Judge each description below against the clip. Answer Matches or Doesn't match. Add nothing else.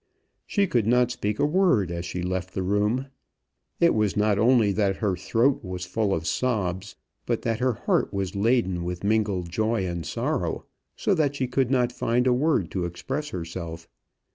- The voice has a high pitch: Doesn't match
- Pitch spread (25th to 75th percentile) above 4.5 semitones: Matches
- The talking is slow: Doesn't match